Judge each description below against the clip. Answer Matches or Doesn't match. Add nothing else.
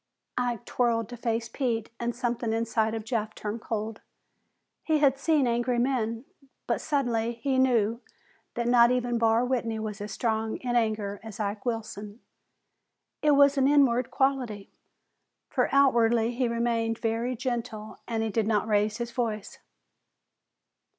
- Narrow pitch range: Matches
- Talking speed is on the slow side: Doesn't match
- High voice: Matches